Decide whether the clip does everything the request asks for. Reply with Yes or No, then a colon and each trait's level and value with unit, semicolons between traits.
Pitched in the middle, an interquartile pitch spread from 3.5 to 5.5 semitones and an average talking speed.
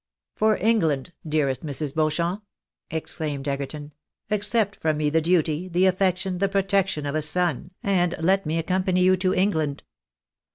Yes: medium, 175 Hz; average, 3.8 semitones; average, 155 wpm